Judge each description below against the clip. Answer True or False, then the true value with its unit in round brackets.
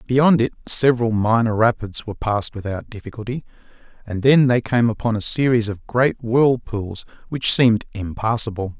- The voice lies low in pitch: True (115 Hz)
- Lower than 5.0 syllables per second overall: False (5.1 syllables/s)